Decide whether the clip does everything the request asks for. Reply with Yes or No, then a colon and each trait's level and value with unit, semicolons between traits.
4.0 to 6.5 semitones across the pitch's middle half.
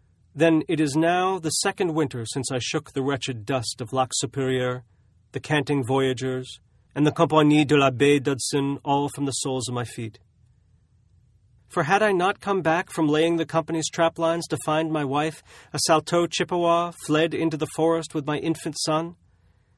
Yes: average, 4.3 semitones